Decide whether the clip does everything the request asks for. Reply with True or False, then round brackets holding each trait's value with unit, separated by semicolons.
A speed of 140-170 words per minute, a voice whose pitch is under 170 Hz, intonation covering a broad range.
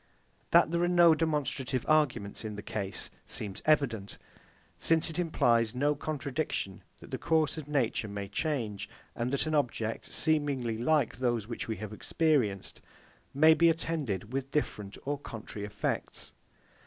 True (150 wpm; 135 Hz; 6.1 semitones)